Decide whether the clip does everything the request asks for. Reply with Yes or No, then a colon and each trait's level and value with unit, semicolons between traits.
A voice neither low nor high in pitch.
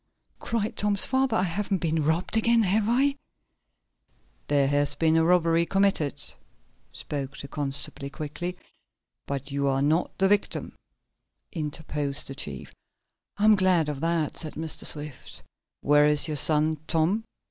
Yes: medium, 160 Hz